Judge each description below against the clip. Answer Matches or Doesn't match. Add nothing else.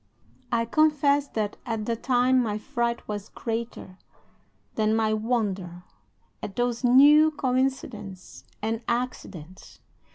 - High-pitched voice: Matches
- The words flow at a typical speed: Doesn't match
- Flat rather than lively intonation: Doesn't match